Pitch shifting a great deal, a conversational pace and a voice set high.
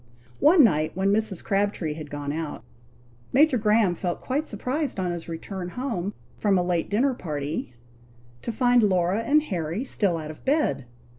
Yes: wide, 6.7 semitones; average, 165 wpm; high, 195 Hz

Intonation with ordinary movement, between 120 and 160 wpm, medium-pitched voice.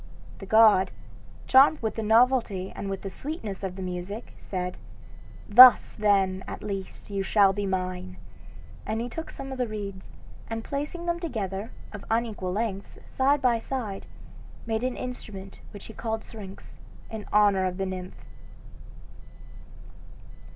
No: average, 3.6 semitones; average, 150 wpm; high, 210 Hz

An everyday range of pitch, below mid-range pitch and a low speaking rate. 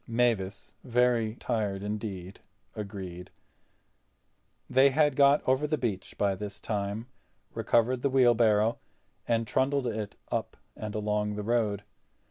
Yes: average, 3.2 semitones; low, 110 Hz; slow, 120 wpm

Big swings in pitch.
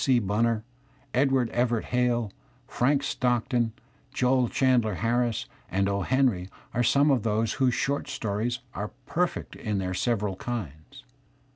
No: average, 3.2 semitones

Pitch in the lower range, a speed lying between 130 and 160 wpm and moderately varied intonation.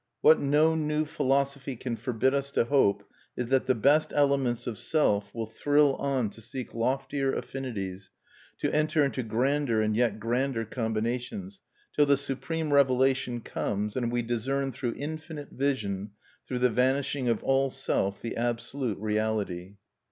Yes: low, 130 Hz; average, 150 wpm; average, 3.6 semitones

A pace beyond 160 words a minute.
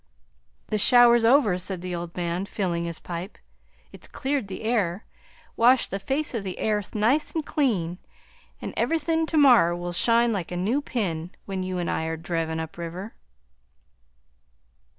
Yes: average, 170 wpm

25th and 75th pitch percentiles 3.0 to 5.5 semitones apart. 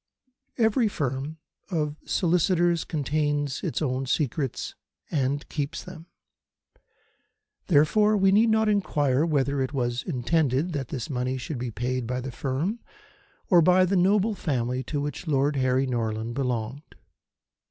Yes: average, 5.2 semitones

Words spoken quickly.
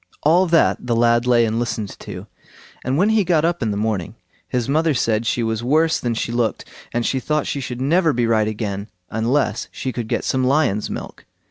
Yes: fast, 215 wpm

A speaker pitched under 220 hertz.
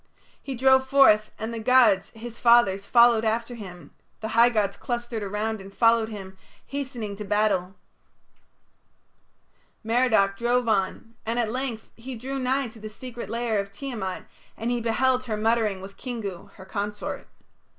No: high, 225 Hz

